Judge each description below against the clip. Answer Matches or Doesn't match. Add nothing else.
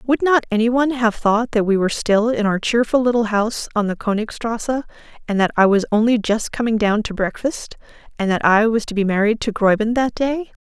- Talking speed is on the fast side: Matches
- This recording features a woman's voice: Matches